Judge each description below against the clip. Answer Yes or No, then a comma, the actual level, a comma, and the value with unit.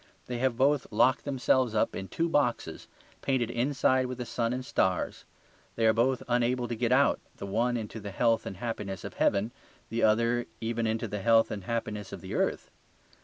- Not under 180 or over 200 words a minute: Yes, average, 195 wpm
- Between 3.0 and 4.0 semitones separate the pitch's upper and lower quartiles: No, narrow, 2.4 semitones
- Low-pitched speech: Yes, low, 115 Hz